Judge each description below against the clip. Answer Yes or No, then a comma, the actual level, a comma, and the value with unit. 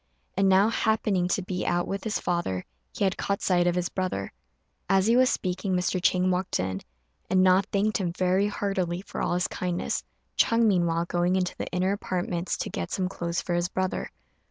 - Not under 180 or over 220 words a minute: Yes, average, 200 wpm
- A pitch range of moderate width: No, narrow, 1.8 semitones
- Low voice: No, medium, 185 Hz